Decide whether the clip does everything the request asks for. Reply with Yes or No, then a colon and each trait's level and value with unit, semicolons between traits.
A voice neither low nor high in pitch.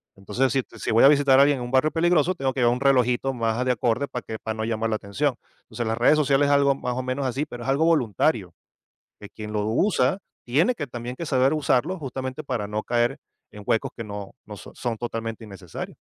No: low, 125 Hz